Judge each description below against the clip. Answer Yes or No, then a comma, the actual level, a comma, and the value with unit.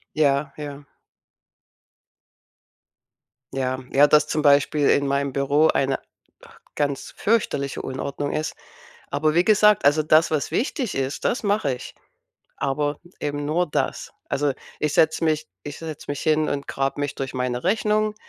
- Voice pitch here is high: No, medium, 145 Hz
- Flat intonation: Yes, narrow, 2.2 semitones